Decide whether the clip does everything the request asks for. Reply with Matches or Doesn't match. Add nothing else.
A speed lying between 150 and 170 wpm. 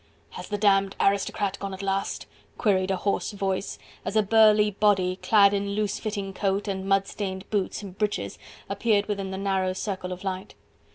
Doesn't match